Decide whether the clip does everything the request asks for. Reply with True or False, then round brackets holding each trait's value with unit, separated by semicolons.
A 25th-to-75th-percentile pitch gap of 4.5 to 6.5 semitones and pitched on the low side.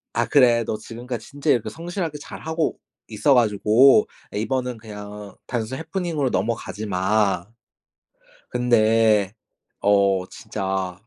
False (4.1 semitones; 115 Hz)